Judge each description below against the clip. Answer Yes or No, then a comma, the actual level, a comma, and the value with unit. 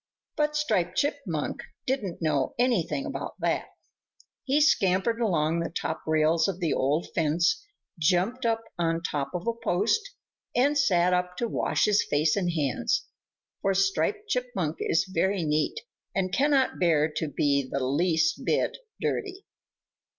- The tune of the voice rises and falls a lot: Yes, wide, 7.1 semitones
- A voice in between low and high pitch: Yes, medium, 180 Hz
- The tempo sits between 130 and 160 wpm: Yes, average, 145 wpm